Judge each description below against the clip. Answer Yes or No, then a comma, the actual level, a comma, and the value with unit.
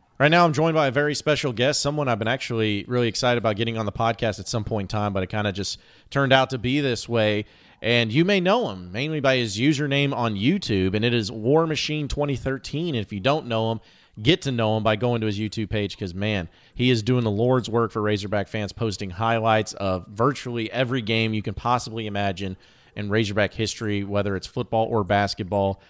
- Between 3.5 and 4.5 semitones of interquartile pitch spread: Yes, average, 3.9 semitones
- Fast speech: Yes, fast, 225 wpm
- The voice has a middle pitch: No, low, 115 Hz